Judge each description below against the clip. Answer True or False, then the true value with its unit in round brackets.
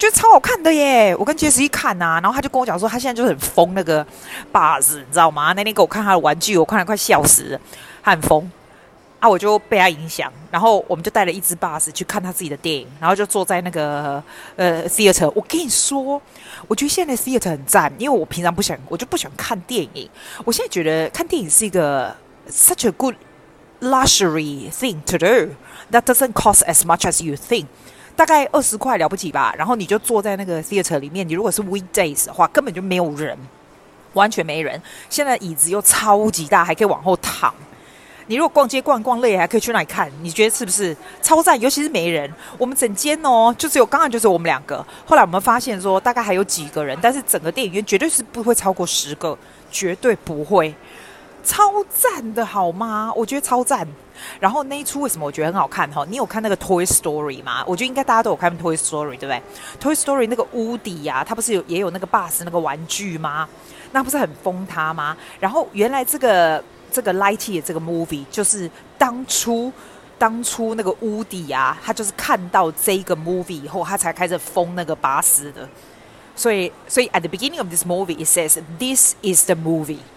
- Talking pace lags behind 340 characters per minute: False (405 characters per minute)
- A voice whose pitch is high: True (195 Hz)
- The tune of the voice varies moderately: False (6.3 semitones)